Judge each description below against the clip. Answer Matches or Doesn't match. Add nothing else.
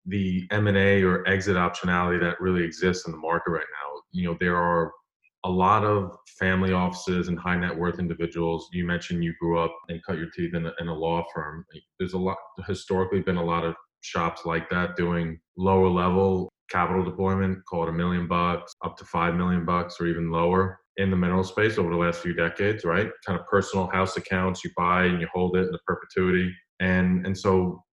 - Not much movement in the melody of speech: Matches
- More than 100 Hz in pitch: Doesn't match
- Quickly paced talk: Matches